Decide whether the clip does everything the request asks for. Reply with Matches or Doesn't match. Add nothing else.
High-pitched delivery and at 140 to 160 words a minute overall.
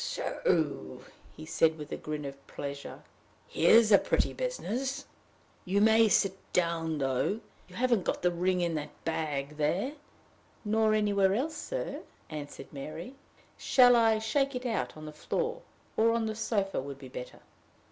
Matches